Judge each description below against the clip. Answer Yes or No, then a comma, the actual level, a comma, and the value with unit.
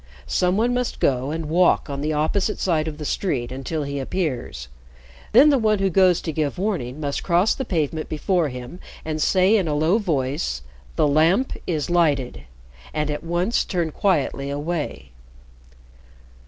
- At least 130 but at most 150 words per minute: No, average, 170 wpm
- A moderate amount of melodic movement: Yes, average, 4.4 semitones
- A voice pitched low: No, medium, 160 Hz